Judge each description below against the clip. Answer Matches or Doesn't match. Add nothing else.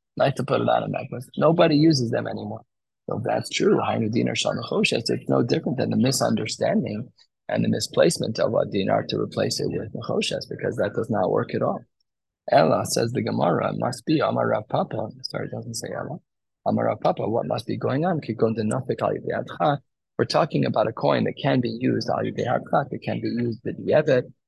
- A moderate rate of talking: Matches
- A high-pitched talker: Doesn't match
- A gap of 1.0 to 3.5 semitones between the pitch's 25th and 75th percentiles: Doesn't match